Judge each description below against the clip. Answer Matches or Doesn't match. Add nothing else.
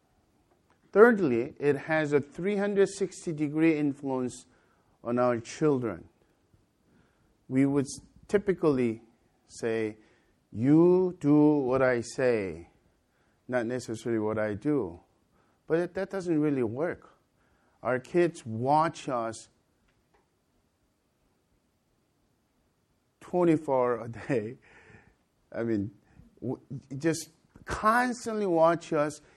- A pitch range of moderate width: Doesn't match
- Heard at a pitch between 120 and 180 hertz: Matches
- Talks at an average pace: Doesn't match